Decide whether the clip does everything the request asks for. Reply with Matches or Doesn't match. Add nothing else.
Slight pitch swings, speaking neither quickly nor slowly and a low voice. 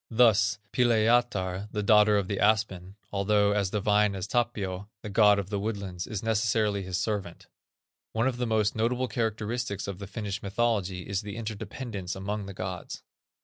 Matches